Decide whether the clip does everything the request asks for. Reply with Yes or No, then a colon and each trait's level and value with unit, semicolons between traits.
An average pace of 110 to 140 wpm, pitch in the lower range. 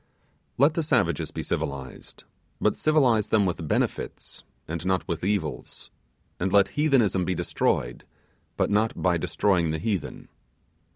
Yes: slow, 135 wpm; very low, 95 Hz